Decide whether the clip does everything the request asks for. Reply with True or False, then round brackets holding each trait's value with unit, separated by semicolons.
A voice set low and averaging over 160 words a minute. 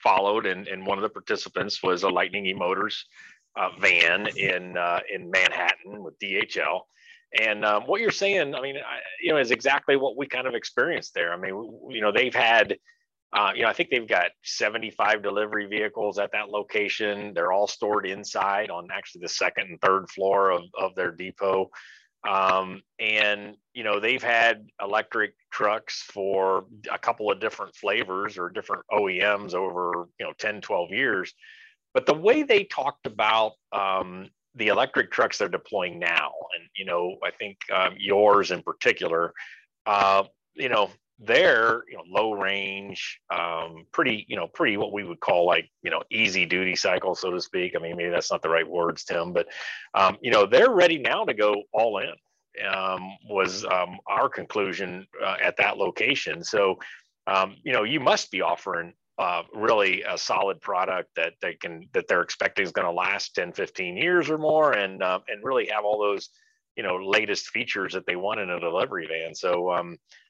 True (105 Hz; 190 wpm)